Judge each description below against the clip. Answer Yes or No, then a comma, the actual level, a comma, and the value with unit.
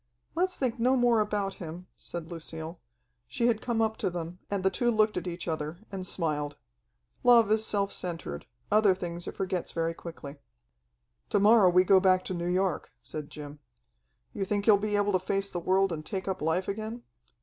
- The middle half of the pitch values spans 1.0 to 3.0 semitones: No, average, 3.9 semitones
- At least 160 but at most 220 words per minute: Yes, average, 195 wpm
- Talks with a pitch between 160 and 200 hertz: Yes, high, 190 Hz